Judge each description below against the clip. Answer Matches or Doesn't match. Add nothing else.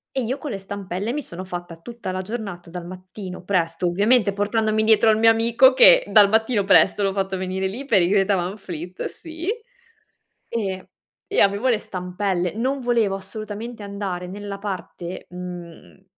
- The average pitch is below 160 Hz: Doesn't match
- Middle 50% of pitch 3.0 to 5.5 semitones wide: Matches